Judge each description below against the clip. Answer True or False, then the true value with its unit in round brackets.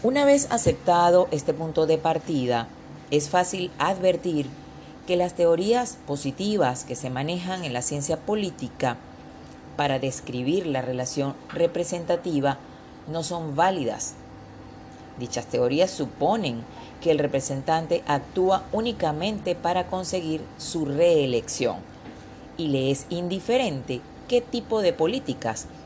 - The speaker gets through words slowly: True (115 wpm)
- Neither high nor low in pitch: True (160 Hz)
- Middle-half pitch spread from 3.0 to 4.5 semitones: False (5.2 semitones)